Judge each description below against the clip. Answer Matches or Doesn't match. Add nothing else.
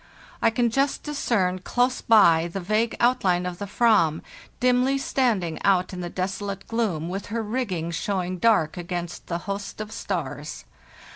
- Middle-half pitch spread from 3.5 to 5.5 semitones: Matches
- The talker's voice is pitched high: Matches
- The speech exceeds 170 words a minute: Doesn't match